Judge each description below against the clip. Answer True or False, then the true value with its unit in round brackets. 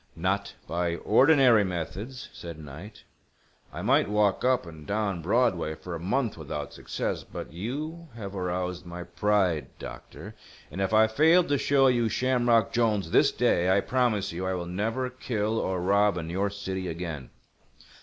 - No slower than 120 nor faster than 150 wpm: False (165 wpm)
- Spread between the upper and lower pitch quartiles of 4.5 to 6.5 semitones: True (4.9 semitones)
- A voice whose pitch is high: False (100 Hz)